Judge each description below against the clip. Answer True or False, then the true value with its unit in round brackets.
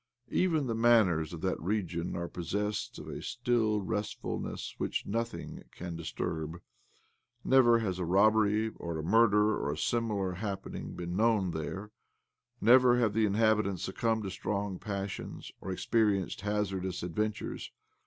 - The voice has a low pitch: True (105 Hz)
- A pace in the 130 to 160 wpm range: True (140 wpm)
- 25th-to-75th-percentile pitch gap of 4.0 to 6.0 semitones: False (3.5 semitones)